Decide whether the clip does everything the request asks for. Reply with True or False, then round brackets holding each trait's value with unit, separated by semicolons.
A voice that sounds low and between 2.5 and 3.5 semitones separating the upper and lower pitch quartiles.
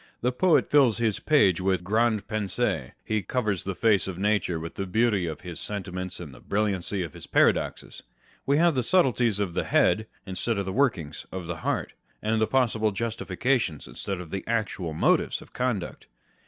False (105 Hz; 4.2 semitones)